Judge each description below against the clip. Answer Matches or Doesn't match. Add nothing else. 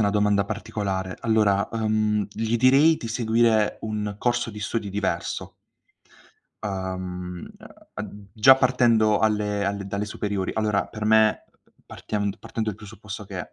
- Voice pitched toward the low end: Matches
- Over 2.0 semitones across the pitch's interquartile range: Doesn't match